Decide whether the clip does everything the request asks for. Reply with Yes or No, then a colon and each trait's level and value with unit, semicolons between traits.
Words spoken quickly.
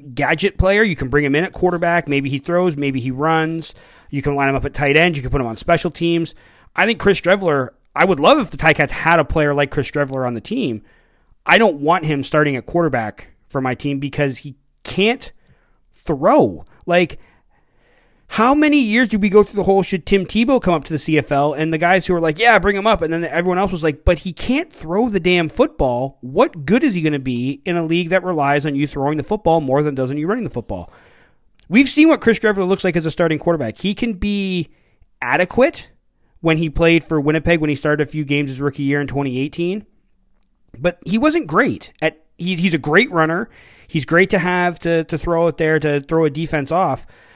Yes: fast, 230 wpm